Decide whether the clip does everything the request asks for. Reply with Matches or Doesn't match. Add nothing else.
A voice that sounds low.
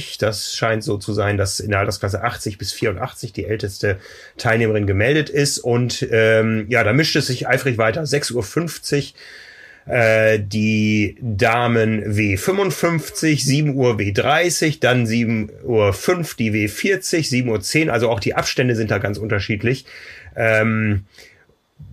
Matches